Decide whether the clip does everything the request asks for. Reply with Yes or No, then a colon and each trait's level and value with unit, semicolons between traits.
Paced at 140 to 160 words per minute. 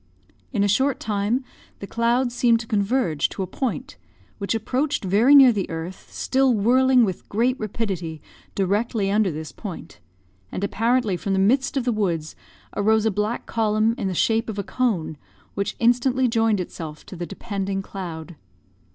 No: average, 170 wpm